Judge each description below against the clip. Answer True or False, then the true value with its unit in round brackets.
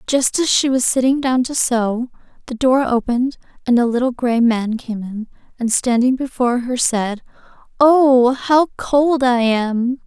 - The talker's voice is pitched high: True (250 Hz)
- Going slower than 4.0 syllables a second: False (4.2 syllables/s)